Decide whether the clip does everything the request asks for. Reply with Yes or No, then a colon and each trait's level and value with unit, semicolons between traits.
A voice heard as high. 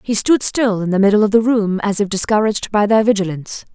Yes: high, 210 Hz